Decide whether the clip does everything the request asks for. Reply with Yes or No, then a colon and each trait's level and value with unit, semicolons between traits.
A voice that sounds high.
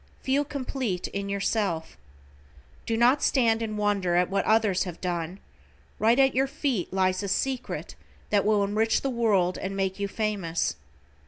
Yes: high, 205 Hz